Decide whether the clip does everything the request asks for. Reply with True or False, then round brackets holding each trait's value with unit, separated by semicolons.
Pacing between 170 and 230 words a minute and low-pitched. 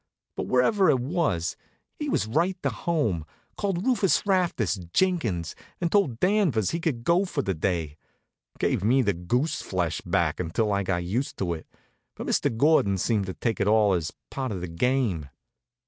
True (180 wpm; 115 Hz)